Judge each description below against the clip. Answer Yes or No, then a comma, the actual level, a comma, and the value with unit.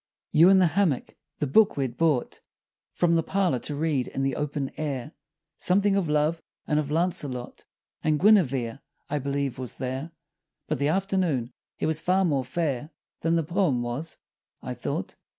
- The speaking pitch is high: No, medium, 150 Hz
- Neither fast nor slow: Yes, average, 170 wpm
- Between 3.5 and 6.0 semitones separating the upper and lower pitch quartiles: Yes, average, 4.3 semitones